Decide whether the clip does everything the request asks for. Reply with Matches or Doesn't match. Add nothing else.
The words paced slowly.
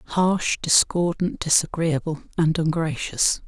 Matches